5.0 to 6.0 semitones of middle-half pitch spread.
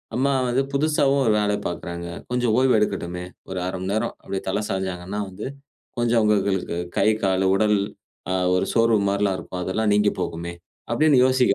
No: average, 4.1 semitones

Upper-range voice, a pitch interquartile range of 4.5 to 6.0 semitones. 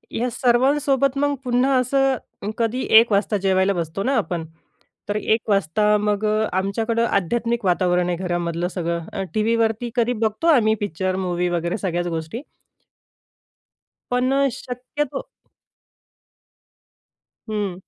Yes: high, 210 Hz; average, 4.9 semitones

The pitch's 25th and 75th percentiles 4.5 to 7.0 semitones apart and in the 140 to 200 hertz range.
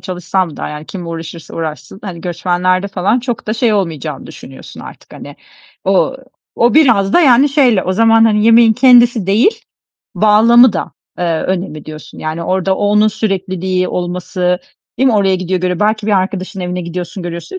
No: average, 3.7 semitones; high, 190 Hz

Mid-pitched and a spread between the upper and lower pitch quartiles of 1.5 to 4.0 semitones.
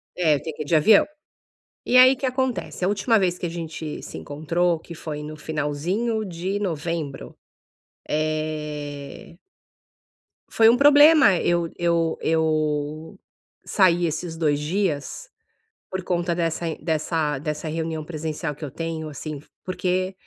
Yes: medium, 165 Hz; average, 3.3 semitones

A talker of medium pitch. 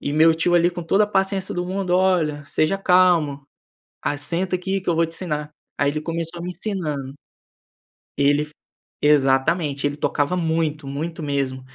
Yes: medium, 165 Hz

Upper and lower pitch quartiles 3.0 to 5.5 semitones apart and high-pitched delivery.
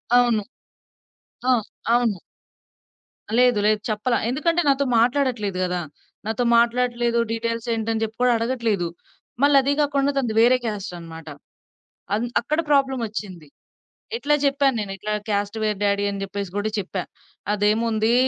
Yes: average, 3.5 semitones; high, 230 Hz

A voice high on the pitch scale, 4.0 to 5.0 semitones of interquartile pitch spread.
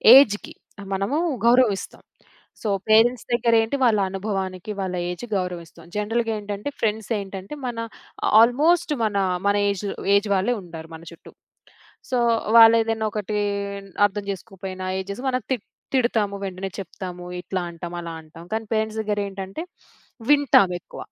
No: high, 205 Hz; average, 3.4 semitones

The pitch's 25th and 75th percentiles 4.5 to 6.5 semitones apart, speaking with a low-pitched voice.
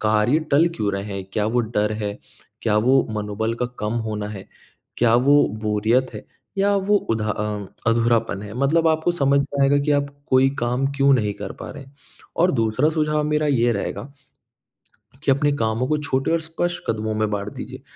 Yes: average, 5.0 semitones; low, 120 Hz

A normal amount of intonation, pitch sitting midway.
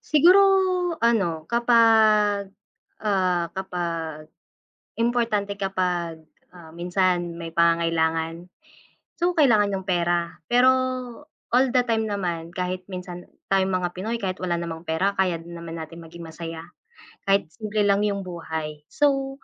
Yes: average, 3.8 semitones; medium, 180 Hz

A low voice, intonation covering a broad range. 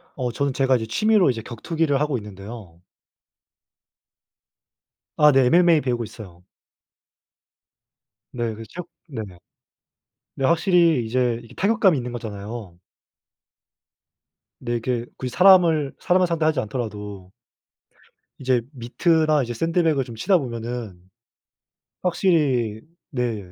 Yes: low, 125 Hz; wide, 6.0 semitones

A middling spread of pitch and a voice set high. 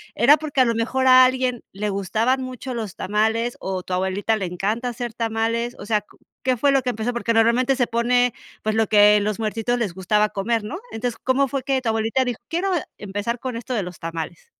Yes: average, 3.2 semitones; high, 230 Hz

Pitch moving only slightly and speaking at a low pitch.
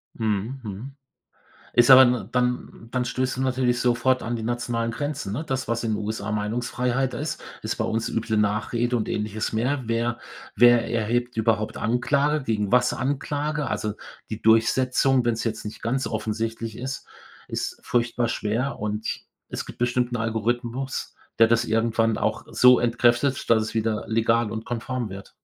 Yes: narrow, 2.2 semitones; low, 120 Hz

